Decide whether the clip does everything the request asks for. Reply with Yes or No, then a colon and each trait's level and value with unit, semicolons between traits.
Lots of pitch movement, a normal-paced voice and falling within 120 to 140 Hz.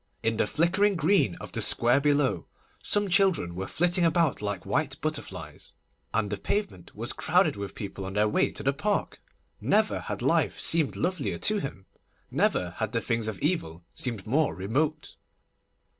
Yes: wide, 8.9 semitones; average, 170 wpm; low, 135 Hz